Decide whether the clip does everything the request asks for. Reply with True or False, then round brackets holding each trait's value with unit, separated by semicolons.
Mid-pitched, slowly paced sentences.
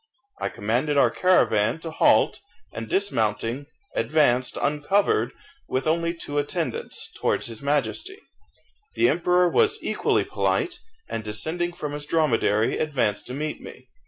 True (145 Hz; 130 wpm)